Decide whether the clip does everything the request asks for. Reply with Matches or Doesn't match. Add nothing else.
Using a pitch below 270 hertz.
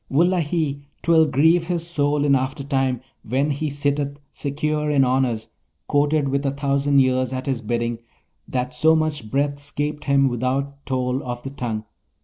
Matches